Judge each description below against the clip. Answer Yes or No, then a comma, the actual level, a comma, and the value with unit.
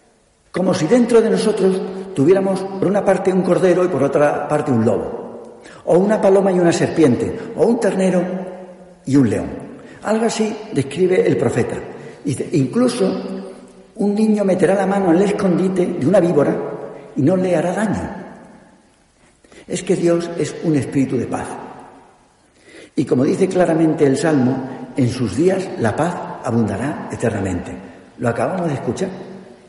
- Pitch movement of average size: No, wide, 6.3 semitones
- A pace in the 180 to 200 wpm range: No, average, 155 wpm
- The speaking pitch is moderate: Yes, medium, 180 Hz